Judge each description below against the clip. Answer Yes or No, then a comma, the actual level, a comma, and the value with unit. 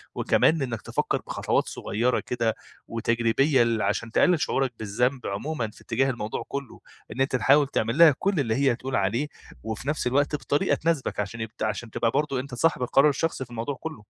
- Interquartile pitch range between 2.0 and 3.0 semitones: No, average, 3.8 semitones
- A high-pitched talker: No, low, 125 Hz